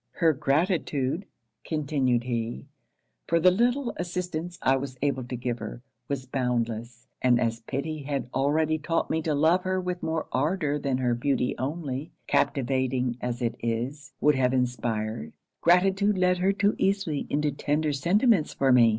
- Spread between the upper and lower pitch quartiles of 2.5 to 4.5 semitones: No, average, 5.1 semitones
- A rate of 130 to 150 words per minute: No, average, 160 wpm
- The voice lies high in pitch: No, medium, 140 Hz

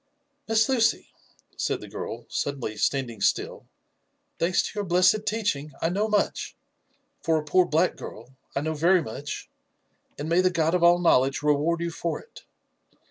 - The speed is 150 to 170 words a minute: No, average, 185 wpm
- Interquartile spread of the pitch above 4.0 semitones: Yes, average, 4.9 semitones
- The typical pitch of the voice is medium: Yes, medium, 170 Hz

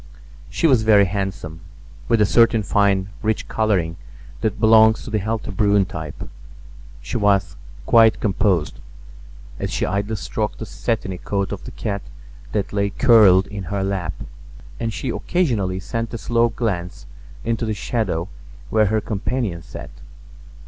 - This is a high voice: No, low, 105 Hz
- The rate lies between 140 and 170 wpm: Yes, average, 150 wpm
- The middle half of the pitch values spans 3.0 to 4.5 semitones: No, narrow, 2.6 semitones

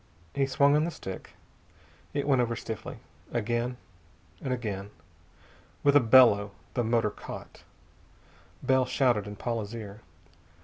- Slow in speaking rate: Yes, slow, 130 wpm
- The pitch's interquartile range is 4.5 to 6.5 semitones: No, average, 3.7 semitones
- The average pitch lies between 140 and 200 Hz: No, low, 120 Hz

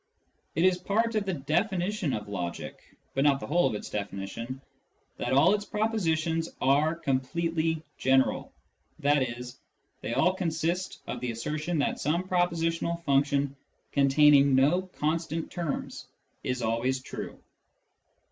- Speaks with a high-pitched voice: No, medium, 155 Hz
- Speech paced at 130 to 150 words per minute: Yes, slow, 135 wpm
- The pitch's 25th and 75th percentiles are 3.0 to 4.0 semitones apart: No, average, 4.6 semitones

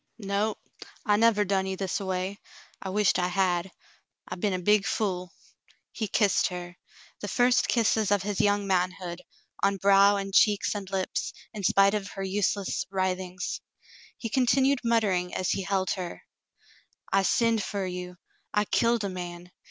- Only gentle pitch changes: Yes, narrow, 2.1 semitones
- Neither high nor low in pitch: No, high, 195 Hz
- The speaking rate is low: No, average, 165 wpm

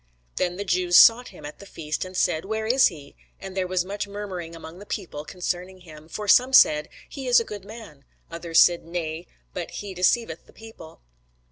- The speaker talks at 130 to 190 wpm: No, fast, 205 wpm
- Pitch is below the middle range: No, medium, 185 Hz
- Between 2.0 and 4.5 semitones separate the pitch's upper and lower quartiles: Yes, average, 3.8 semitones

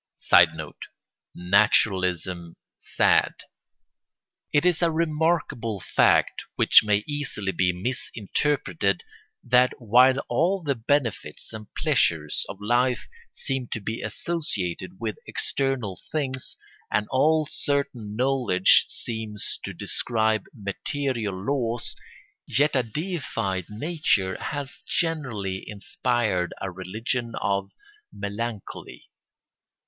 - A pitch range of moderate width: No, wide, 5.8 semitones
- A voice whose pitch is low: Yes, low, 115 Hz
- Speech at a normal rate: No, slow, 100 wpm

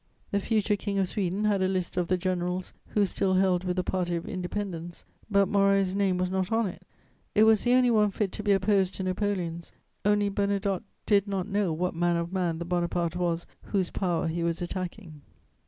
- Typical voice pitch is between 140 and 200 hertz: Yes, medium, 185 Hz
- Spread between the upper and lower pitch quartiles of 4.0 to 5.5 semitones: No, narrow, 2.4 semitones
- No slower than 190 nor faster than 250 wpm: Yes, fast, 205 wpm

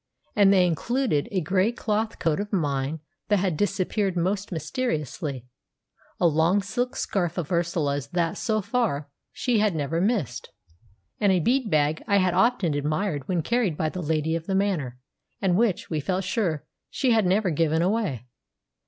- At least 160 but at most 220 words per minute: Yes, average, 170 wpm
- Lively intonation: No, average, 4.8 semitones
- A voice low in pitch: No, medium, 180 Hz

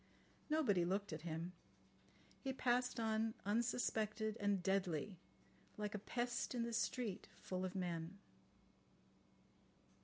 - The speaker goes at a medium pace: No, slow, 115 wpm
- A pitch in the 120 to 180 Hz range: No, high, 210 Hz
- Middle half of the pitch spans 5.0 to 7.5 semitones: No, average, 4.2 semitones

